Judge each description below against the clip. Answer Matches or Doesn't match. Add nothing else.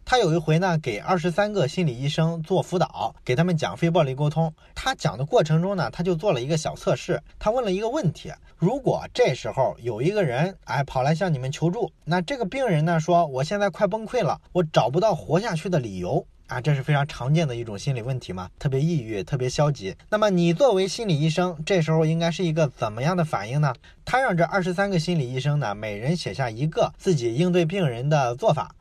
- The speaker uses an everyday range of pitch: Matches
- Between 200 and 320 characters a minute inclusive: Doesn't match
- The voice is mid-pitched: Matches